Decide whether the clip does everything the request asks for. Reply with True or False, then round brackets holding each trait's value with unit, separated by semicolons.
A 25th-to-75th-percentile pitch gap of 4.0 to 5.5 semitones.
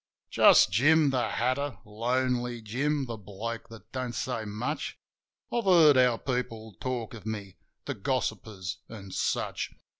False (3.2 semitones)